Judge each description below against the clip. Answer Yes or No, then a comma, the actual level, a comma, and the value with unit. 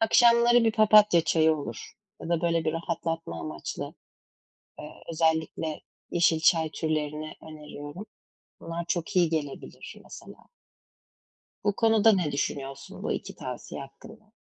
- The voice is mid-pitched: Yes, medium, 165 Hz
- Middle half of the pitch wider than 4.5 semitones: Yes, average, 5.0 semitones